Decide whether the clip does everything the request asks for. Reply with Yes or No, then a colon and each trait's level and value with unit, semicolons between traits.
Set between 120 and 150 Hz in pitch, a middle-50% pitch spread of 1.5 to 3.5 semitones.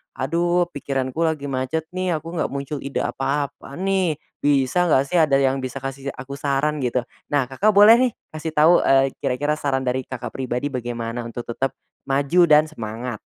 Yes: medium, 140 Hz; average, 3.2 semitones